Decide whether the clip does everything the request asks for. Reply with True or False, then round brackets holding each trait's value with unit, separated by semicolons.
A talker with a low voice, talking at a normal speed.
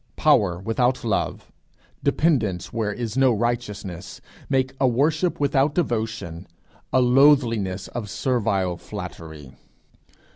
False (115 Hz; 105 wpm)